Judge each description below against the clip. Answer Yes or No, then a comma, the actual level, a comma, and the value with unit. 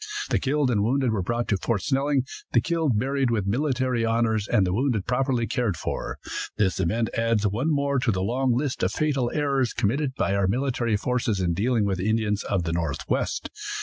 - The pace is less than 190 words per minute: No, average, 200 wpm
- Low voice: Yes, low, 115 Hz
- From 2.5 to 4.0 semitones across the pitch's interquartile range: No, average, 4.5 semitones